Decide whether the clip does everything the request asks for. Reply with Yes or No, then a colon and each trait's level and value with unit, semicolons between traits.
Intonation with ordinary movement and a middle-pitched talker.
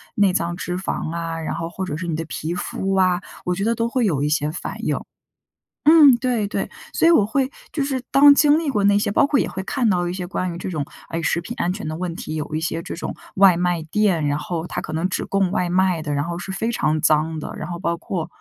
Yes: average, 4.2 semitones; medium, 180 Hz